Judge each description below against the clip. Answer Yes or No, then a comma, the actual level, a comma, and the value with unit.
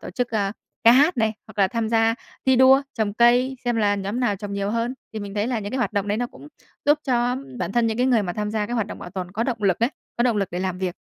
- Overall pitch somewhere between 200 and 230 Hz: Yes, high, 225 Hz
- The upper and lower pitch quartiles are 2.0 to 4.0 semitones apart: Yes, average, 3.2 semitones